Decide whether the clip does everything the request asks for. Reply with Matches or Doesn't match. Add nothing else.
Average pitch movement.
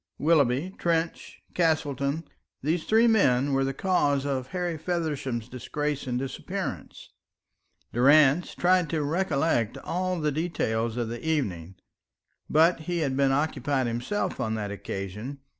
Matches